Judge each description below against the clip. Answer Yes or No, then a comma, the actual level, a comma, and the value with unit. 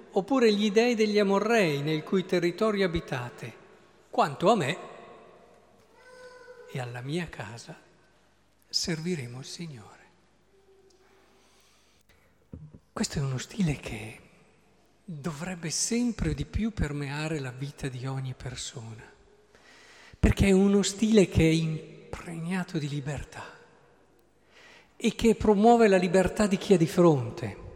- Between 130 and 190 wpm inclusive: No, slow, 115 wpm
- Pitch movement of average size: No, wide, 6.7 semitones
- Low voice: No, medium, 180 Hz